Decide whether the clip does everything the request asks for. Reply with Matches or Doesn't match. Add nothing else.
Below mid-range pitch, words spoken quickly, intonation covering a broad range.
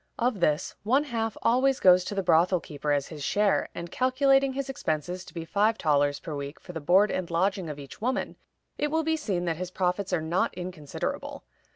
Doesn't match